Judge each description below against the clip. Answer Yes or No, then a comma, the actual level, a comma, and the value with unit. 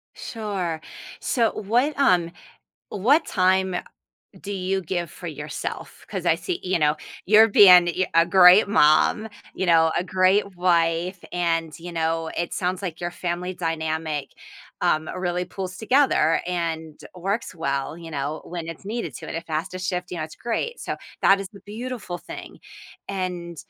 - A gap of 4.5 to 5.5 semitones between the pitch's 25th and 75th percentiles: No, average, 2.9 semitones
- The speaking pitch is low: No, medium, 180 Hz